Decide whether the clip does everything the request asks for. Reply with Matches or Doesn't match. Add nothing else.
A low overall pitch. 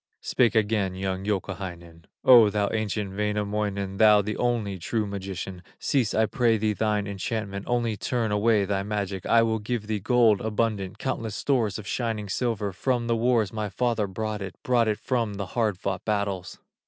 Matches